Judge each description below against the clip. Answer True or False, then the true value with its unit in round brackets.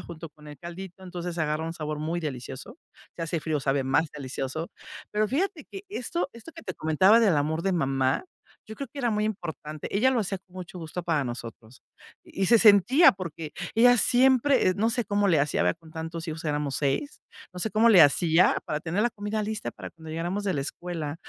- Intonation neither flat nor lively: False (5.8 semitones)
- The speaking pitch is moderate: True (175 Hz)